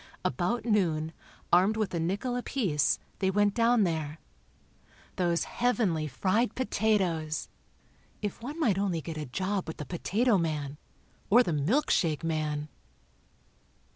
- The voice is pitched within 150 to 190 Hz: Yes, medium, 185 Hz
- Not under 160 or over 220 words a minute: No, slow, 135 wpm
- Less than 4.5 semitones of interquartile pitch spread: No, wide, 5.6 semitones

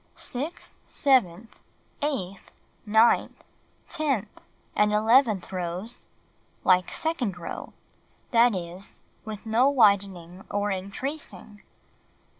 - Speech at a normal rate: No, slow, 90 wpm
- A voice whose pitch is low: No, high, 210 Hz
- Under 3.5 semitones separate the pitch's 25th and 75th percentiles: No, average, 4.8 semitones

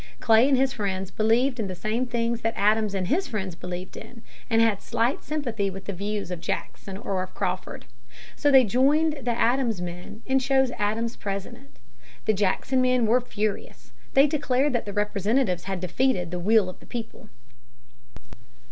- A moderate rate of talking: Yes, average, 175 wpm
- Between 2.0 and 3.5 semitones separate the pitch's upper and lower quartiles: No, average, 4.6 semitones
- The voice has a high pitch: Yes, high, 220 Hz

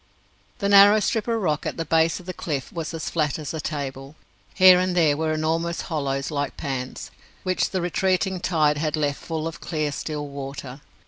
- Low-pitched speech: No, medium, 160 Hz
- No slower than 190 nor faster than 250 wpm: Yes, average, 195 wpm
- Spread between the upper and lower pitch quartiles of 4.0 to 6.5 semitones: No, average, 3.6 semitones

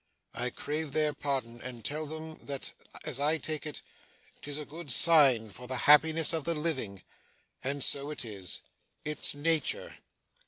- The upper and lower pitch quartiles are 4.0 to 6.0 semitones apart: No, average, 3.6 semitones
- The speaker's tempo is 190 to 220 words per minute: No, average, 160 wpm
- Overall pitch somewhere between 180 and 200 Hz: No, medium, 145 Hz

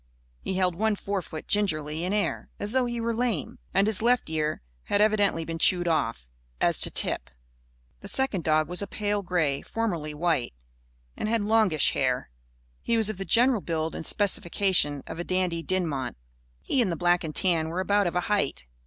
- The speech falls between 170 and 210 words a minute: Yes, average, 190 wpm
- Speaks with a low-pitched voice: No, medium, 185 Hz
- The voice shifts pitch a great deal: No, average, 4.6 semitones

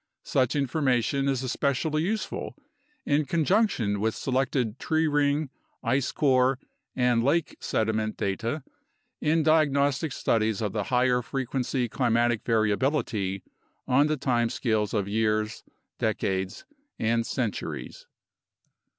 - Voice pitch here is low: Yes, low, 125 Hz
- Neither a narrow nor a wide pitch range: Yes, average, 4.3 semitones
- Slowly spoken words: Yes, slow, 110 wpm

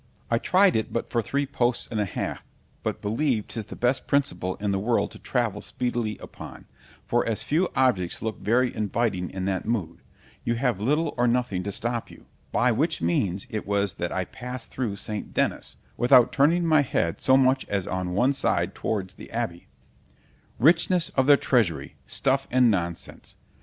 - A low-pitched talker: Yes, low, 115 Hz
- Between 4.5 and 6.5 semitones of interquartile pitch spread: Yes, average, 4.8 semitones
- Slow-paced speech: No, average, 180 wpm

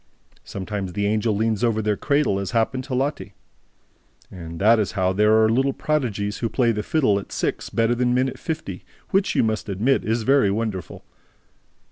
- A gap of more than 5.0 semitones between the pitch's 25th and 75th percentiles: No, average, 3.8 semitones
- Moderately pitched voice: No, low, 110 Hz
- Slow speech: No, average, 185 wpm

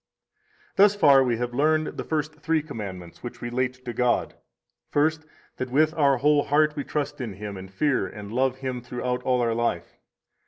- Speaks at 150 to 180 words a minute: No, average, 190 wpm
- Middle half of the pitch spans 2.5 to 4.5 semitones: Yes, average, 3.9 semitones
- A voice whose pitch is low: Yes, low, 130 Hz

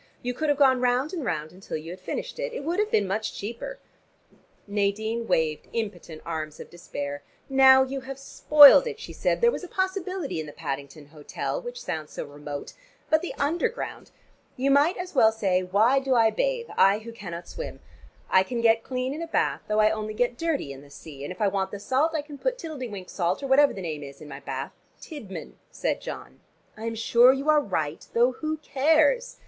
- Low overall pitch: No, high, 235 Hz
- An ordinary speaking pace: No, fast, 220 wpm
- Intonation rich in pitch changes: Yes, wide, 8.4 semitones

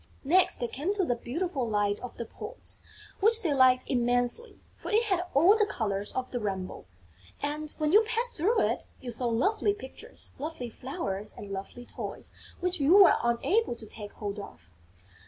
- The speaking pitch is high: Yes, very high, 260 Hz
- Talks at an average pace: Yes, average, 180 wpm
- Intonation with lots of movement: Yes, wide, 8.4 semitones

